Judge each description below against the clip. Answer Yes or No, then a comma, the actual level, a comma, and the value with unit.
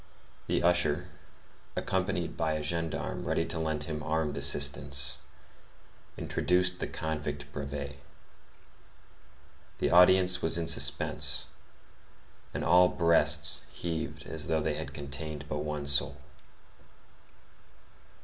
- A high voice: No, very low, 80 Hz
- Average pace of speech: No, slow, 110 wpm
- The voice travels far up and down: No, average, 2.7 semitones